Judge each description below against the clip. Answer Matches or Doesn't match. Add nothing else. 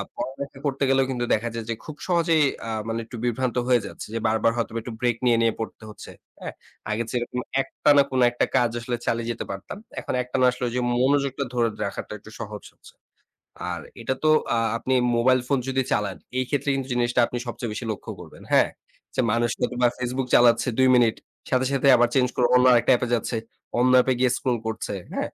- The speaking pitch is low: Matches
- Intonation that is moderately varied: Doesn't match